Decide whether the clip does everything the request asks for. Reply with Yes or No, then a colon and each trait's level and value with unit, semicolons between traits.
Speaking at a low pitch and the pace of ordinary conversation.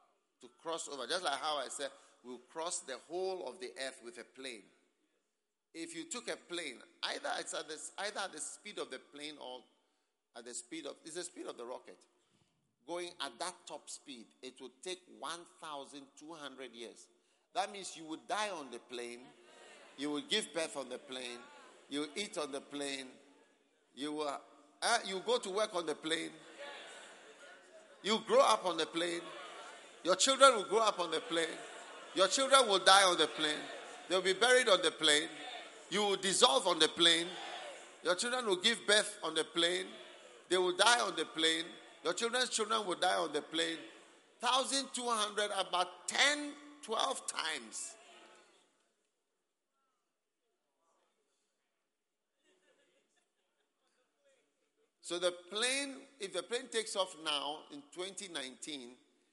No: medium, 175 Hz; average, 160 wpm